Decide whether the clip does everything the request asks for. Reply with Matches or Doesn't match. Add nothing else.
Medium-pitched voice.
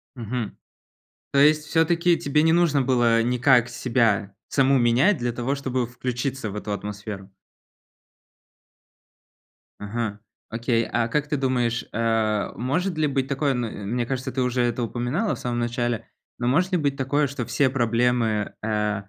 Doesn't match